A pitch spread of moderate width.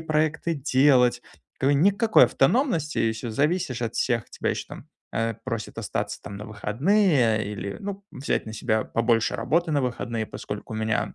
No: wide, 5.8 semitones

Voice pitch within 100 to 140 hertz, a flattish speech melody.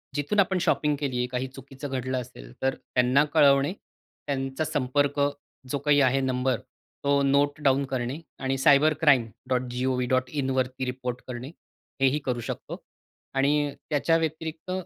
Yes: low, 135 Hz; narrow, 2.1 semitones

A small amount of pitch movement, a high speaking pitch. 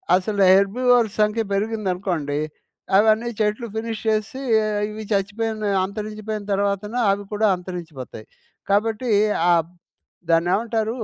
Yes: narrow, 2.3 semitones; high, 210 Hz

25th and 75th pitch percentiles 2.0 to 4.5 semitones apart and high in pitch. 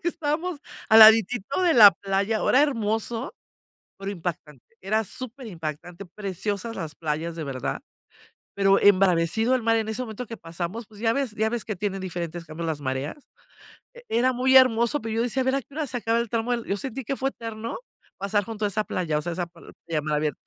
No: wide, 5.4 semitones; high, 215 Hz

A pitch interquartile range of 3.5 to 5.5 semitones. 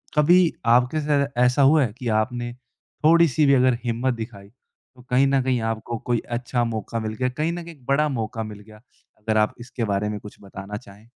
Yes: average, 4.1 semitones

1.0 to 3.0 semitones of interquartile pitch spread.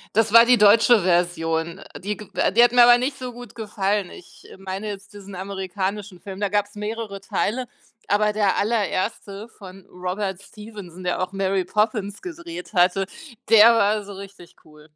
Yes: narrow, 2.5 semitones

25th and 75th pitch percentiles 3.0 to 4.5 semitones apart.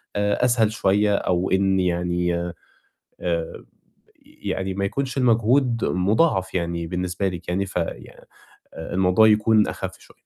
Yes: average, 3.6 semitones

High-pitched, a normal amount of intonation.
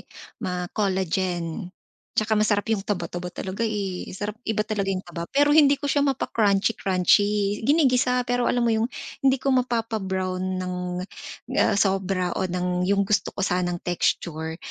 Yes: high, 200 Hz; average, 3.6 semitones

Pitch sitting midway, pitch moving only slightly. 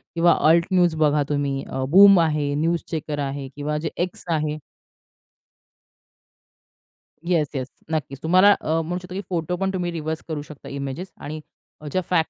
No: medium, 160 Hz; average, 3.1 semitones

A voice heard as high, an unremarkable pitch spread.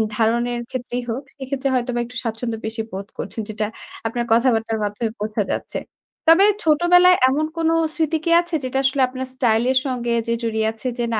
Yes: high, 245 Hz; average, 3.3 semitones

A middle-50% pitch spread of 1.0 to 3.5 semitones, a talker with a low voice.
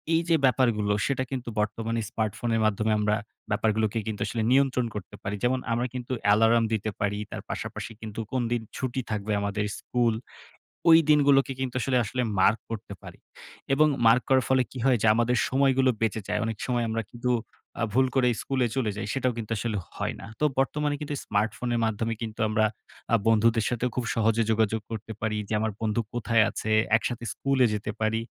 Yes: average, 2.8 semitones; low, 115 Hz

